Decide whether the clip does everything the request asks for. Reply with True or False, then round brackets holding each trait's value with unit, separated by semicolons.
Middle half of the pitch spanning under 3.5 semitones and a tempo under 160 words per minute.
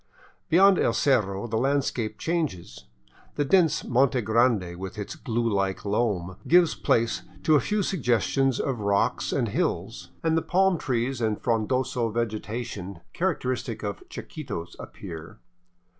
False (5.3 semitones; 140 wpm)